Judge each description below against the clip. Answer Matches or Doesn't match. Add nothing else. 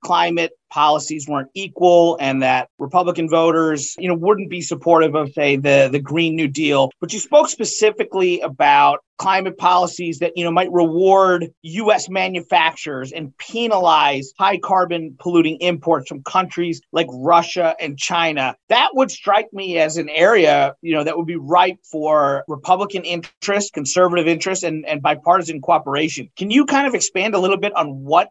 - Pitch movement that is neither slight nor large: Matches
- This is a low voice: Doesn't match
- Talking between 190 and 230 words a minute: Doesn't match